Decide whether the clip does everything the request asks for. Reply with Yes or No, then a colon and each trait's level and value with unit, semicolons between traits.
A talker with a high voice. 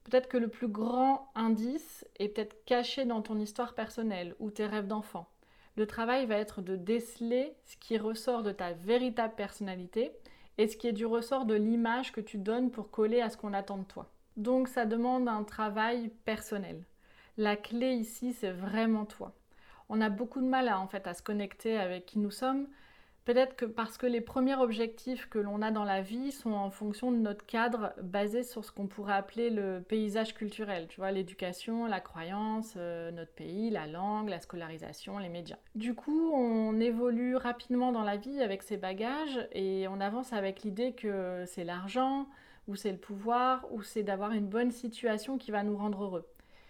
Yes: high, 220 Hz